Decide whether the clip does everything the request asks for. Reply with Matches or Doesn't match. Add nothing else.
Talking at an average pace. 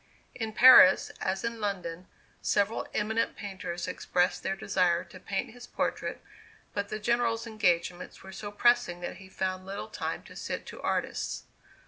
Matches